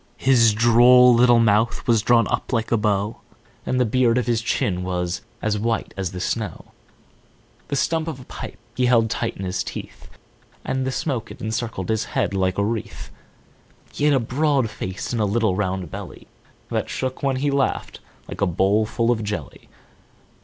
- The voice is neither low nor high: No, low, 115 Hz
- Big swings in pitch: No, average, 3.5 semitones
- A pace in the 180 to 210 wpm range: Yes, average, 185 wpm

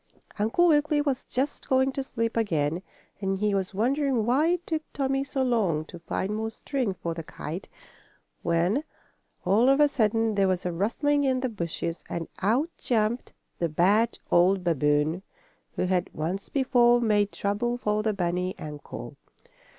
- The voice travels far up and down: Yes, wide, 6.5 semitones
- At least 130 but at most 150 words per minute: No, average, 165 wpm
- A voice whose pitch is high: Yes, high, 215 Hz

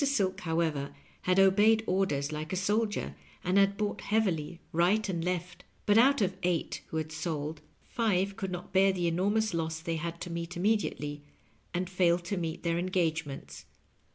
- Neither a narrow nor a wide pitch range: Yes, average, 3.2 semitones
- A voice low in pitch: No, medium, 180 Hz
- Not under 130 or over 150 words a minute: No, average, 175 wpm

